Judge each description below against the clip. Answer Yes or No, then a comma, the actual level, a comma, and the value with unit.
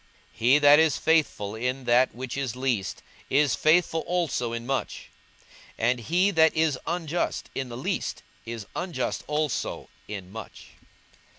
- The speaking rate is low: No, average, 150 wpm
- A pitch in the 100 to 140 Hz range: Yes, low, 135 Hz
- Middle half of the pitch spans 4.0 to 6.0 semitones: Yes, average, 5.1 semitones